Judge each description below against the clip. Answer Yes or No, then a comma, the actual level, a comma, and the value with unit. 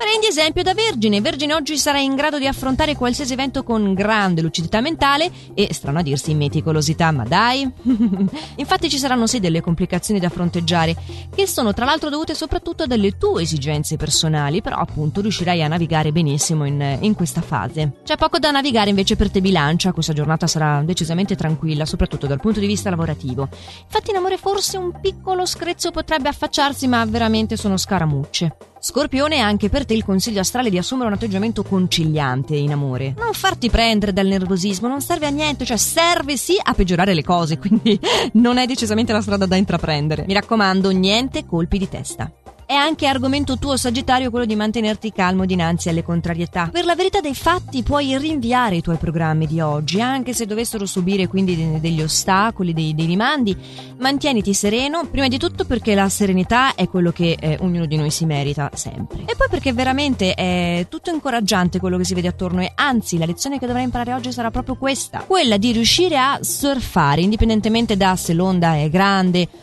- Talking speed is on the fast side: Yes, fast, 185 wpm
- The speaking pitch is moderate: No, high, 205 Hz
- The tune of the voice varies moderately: No, wide, 7.8 semitones